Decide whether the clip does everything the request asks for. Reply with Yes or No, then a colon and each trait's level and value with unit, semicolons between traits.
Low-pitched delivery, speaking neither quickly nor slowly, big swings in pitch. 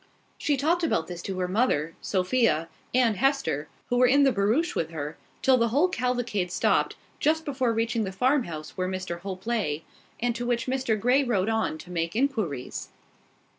No: high, 225 Hz; average, 180 wpm; wide, 6.0 semitones